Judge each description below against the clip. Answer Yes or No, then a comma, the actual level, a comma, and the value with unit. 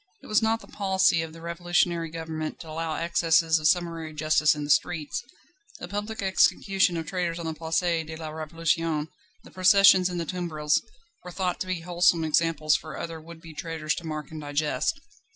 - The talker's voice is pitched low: No, medium, 165 Hz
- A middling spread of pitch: No, narrow, 2.1 semitones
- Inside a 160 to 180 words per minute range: No, average, 190 wpm